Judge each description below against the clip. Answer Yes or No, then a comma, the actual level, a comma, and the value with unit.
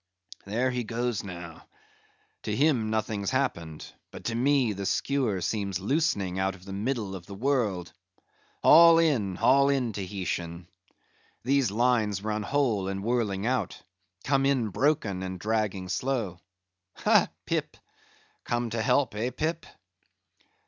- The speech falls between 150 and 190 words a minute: No, slow, 135 wpm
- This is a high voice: No, low, 110 Hz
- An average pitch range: Yes, average, 5.0 semitones